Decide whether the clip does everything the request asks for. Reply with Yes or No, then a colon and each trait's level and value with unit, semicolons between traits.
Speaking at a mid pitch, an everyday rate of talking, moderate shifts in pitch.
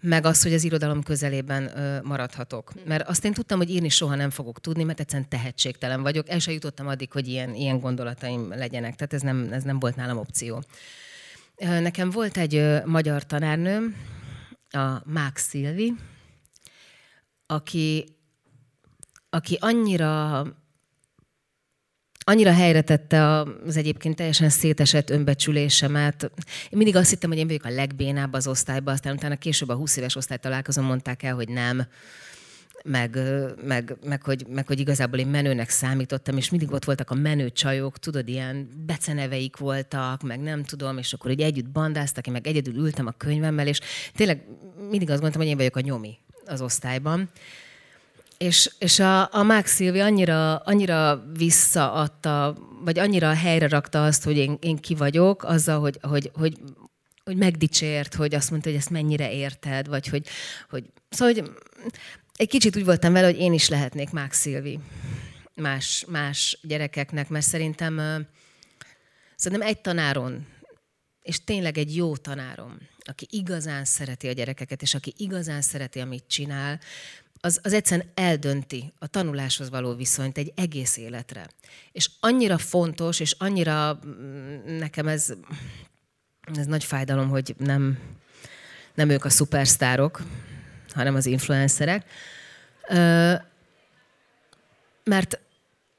Yes: medium, 145 Hz; average, 140 wpm; average, 3.2 semitones